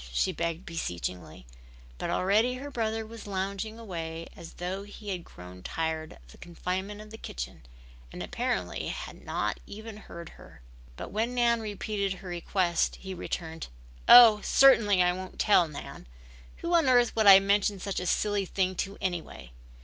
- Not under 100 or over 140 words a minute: No, average, 165 wpm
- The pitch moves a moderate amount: Yes, average, 4.1 semitones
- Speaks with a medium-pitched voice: No, high, 195 Hz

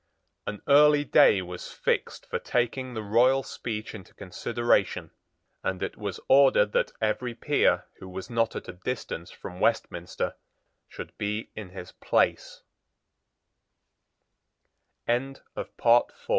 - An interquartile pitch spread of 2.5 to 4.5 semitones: No, average, 4.9 semitones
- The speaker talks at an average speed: No, slow, 115 wpm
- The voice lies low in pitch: Yes, low, 110 Hz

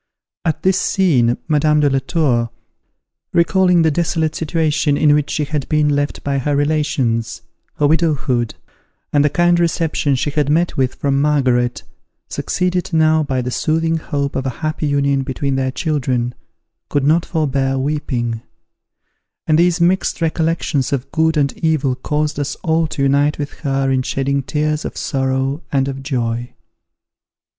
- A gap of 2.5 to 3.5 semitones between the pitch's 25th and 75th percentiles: Yes, average, 3.0 semitones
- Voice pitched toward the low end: No, medium, 145 Hz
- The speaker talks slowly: No, average, 155 wpm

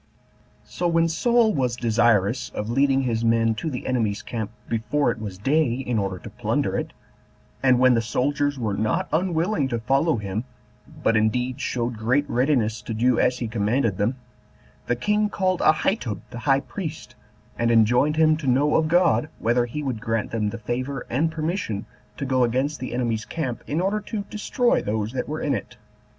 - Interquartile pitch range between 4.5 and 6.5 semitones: Yes, average, 4.8 semitones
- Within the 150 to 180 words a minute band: No, average, 190 wpm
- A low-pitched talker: Yes, low, 125 Hz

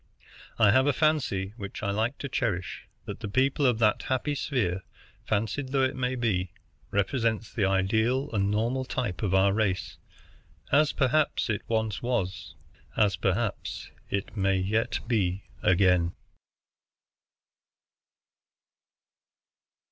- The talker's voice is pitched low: Yes, low, 110 Hz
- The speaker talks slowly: Yes, slow, 125 wpm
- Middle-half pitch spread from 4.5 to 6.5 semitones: Yes, average, 4.8 semitones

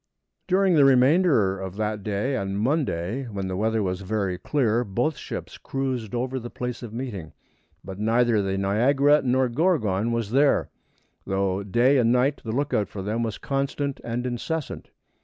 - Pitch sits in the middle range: No, low, 120 Hz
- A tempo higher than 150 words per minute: Yes, average, 165 wpm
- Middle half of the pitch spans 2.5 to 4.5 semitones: No, average, 5.1 semitones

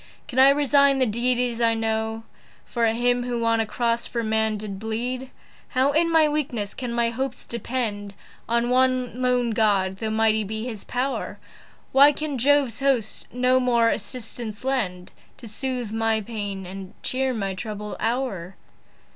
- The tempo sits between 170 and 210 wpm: No, average, 160 wpm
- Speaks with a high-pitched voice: Yes, high, 235 Hz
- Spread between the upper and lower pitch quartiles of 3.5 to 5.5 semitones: No, average, 2.8 semitones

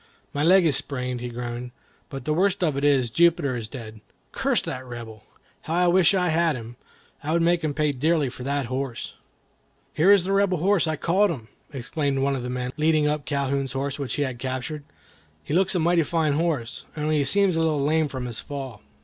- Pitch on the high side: No, medium, 145 Hz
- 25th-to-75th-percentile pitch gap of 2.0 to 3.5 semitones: No, average, 4.4 semitones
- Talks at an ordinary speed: No, fast, 220 wpm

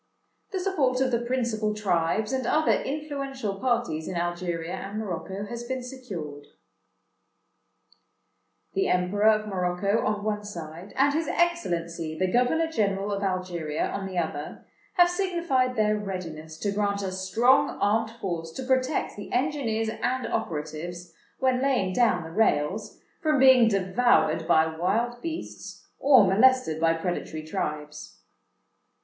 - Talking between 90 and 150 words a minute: Yes, average, 140 wpm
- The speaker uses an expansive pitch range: Yes, wide, 6.5 semitones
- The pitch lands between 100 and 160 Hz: No, high, 210 Hz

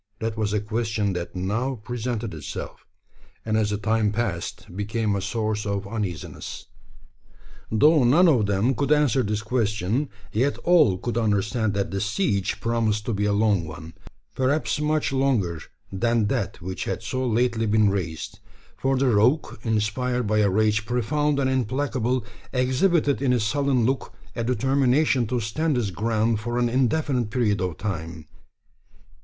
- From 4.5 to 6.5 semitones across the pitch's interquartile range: No, average, 3.8 semitones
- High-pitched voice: No, low, 110 Hz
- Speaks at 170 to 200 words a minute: No, average, 160 wpm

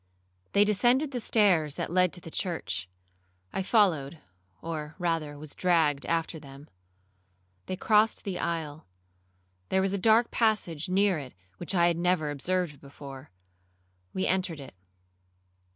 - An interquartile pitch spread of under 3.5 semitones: No, average, 4.4 semitones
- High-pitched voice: No, medium, 170 Hz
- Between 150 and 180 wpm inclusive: No, average, 140 wpm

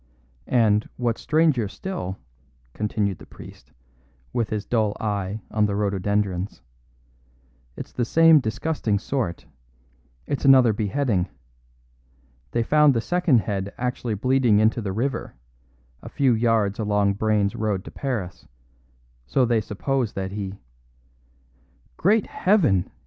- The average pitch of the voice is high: No, low, 110 Hz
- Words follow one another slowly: Yes, slow, 125 wpm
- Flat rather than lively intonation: No, average, 4.2 semitones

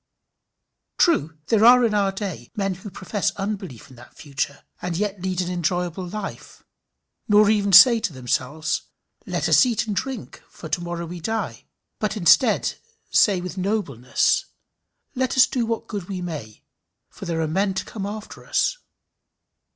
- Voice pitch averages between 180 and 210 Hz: Yes, high, 190 Hz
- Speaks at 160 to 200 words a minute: Yes, average, 165 wpm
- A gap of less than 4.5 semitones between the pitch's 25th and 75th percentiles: Yes, average, 4.0 semitones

